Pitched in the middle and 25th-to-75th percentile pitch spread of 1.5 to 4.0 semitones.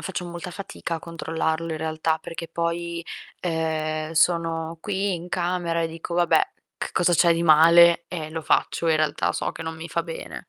No: medium, 165 Hz; narrow, 1.1 semitones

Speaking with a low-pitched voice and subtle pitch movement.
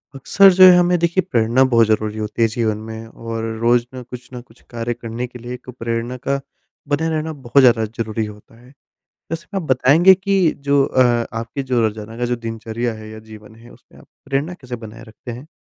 No: low, 120 Hz; average, 3.4 semitones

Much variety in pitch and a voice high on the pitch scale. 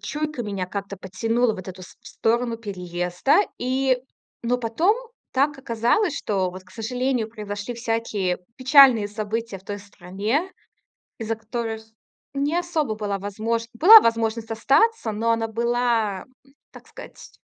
No: average, 3.5 semitones; high, 225 Hz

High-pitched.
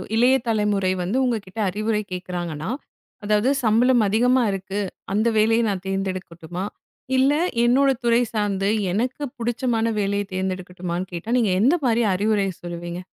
Yes: high, 210 Hz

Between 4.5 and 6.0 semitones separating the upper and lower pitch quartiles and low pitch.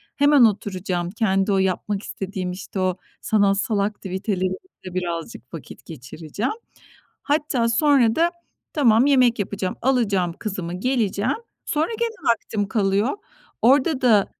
No: average, 4.9 semitones; high, 205 Hz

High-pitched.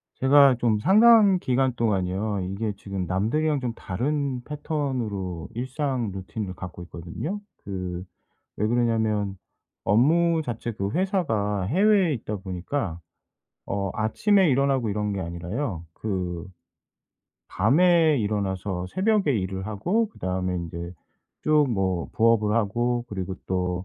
No: low, 110 Hz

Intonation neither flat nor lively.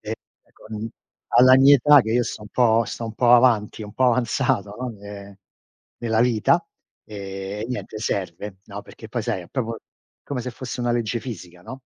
Yes: average, 3.2 semitones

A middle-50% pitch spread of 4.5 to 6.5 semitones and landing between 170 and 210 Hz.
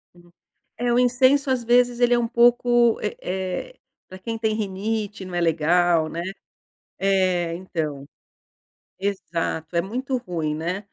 Yes: wide, 5.6 semitones; high, 195 Hz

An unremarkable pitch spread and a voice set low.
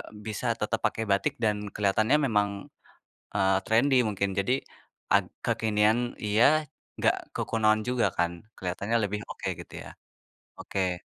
No: narrow, 2.3 semitones; low, 105 Hz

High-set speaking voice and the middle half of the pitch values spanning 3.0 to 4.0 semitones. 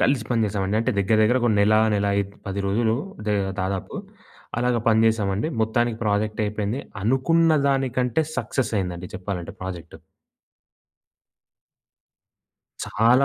No: low, 110 Hz; average, 3.4 semitones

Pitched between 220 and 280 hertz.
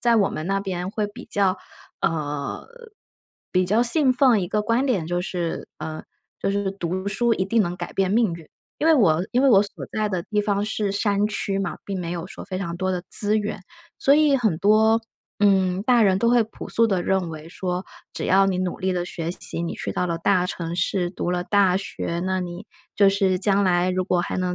No: high, 195 Hz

